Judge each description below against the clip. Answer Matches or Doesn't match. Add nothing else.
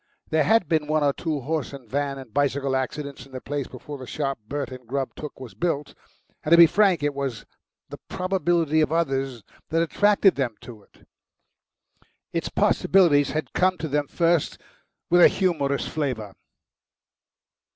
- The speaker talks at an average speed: Matches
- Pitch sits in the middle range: Matches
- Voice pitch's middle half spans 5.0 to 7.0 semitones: Doesn't match